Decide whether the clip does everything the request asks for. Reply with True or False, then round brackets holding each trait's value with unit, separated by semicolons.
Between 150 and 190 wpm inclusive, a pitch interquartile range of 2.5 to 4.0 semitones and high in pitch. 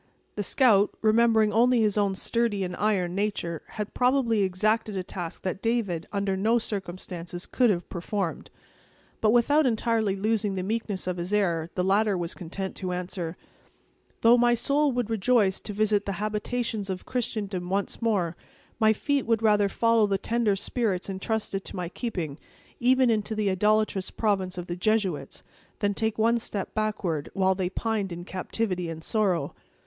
True (165 wpm; 3.3 semitones; 205 Hz)